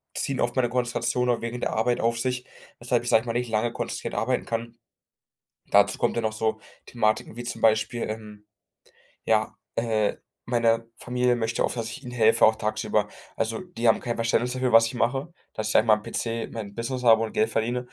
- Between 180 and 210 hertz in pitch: No, low, 115 Hz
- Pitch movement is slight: Yes, narrow, 1.7 semitones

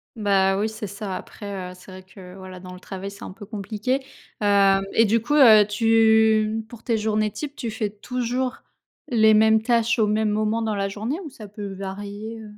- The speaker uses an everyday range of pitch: No, narrow, 2.0 semitones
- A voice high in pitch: Yes, high, 215 Hz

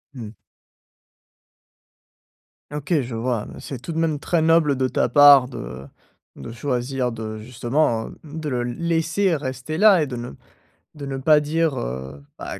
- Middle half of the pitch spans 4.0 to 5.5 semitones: Yes, average, 4.6 semitones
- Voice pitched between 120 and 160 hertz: Yes, low, 135 Hz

